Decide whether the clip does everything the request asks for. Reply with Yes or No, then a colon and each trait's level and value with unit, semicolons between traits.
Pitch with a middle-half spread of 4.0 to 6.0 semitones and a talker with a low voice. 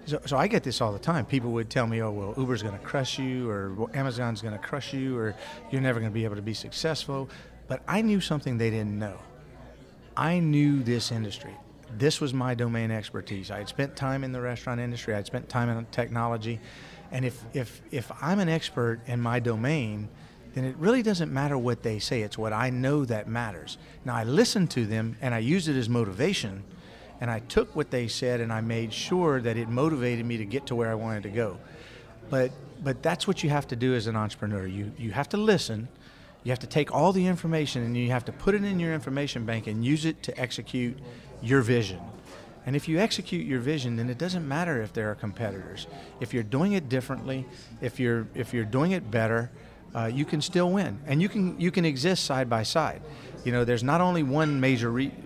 Yes: average, 4.3 semitones; low, 125 Hz